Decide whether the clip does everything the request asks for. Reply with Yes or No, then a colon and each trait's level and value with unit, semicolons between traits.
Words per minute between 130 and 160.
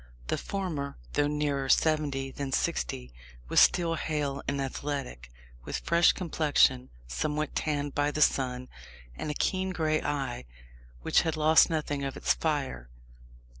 Yes: average, 140 wpm